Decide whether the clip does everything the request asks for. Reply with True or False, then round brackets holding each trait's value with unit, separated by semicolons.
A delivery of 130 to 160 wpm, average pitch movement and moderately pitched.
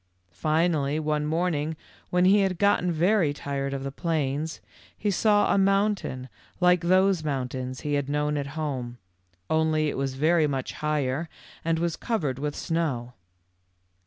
True (150 wpm; 3.9 semitones; 155 Hz)